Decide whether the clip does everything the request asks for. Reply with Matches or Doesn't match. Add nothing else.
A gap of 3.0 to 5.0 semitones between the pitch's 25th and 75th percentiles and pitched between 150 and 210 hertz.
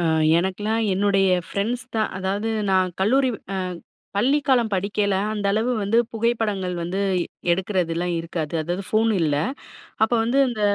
Matches